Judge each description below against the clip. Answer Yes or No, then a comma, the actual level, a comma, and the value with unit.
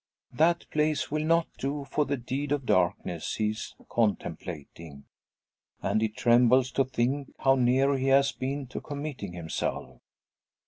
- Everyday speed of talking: Yes, average, 145 wpm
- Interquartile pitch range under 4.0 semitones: No, average, 4.6 semitones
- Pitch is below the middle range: Yes, low, 130 Hz